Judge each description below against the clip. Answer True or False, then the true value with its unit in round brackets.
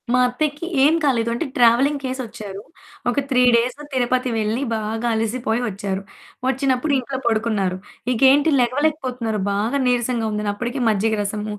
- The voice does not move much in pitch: False (3.2 semitones)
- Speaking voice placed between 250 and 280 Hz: False (240 Hz)